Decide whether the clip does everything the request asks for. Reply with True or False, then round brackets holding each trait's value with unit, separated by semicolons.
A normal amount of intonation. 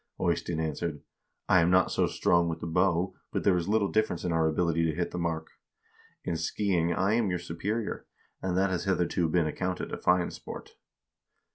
False (2.0 semitones)